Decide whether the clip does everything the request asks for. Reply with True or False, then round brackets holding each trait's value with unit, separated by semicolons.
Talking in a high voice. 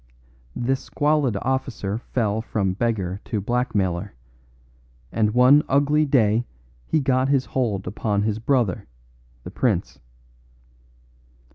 False (115 Hz)